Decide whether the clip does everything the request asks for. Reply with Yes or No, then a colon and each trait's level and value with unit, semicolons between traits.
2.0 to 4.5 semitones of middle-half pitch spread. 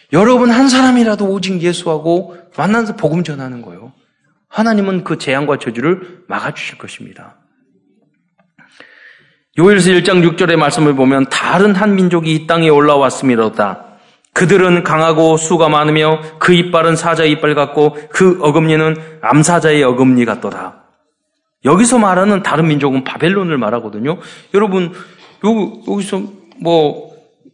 Yes: average, 4.2 semitones